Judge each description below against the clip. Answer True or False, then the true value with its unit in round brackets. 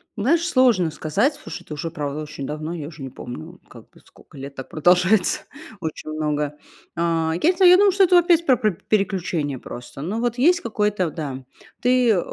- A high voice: False (175 Hz)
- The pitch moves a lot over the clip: True (8.7 semitones)